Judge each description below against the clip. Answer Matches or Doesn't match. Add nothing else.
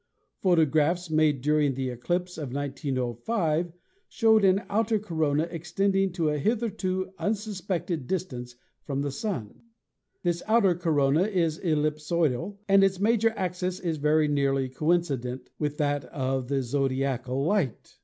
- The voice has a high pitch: Doesn't match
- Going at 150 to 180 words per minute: Doesn't match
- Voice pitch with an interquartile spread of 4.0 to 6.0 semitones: Matches